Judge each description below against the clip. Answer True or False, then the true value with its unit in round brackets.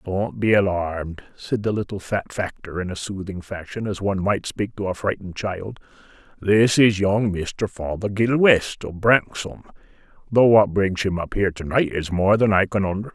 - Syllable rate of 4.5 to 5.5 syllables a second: True (5.0 syllables/s)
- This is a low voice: True (100 Hz)